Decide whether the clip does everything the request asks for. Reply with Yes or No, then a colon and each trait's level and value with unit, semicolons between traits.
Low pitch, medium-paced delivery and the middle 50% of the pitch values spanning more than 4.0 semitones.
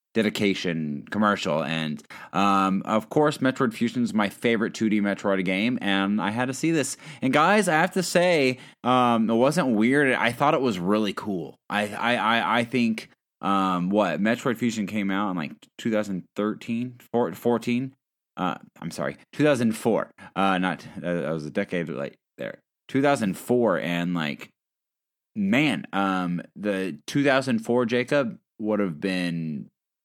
Yes: low, 105 Hz; average, 150 wpm; average, 4.6 semitones